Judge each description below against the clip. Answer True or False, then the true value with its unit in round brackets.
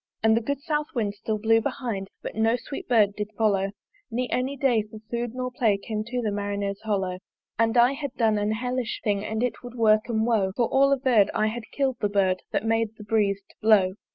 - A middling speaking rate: False (225 wpm)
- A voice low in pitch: False (220 Hz)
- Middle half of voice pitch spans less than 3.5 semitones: True (2.9 semitones)